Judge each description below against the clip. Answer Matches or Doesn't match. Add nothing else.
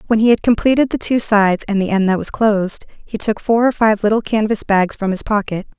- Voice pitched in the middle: Doesn't match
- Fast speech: Matches